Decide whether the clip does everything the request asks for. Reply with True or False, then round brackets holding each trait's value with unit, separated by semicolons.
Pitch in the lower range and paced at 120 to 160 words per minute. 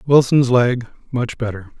True (120 Hz; 135 wpm)